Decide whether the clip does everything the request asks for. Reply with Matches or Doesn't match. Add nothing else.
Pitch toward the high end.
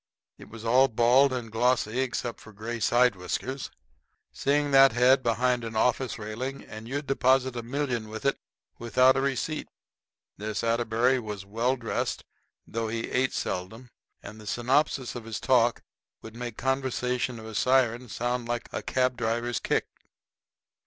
Doesn't match